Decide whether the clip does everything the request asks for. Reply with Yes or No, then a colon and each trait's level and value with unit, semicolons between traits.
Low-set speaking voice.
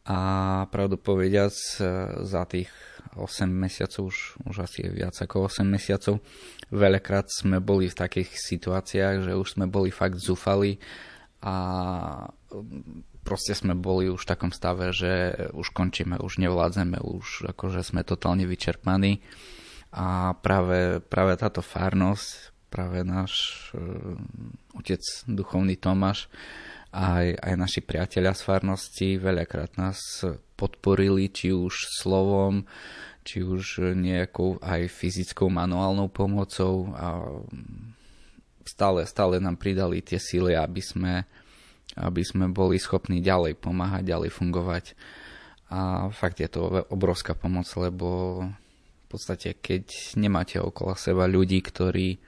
Yes: very low, 95 Hz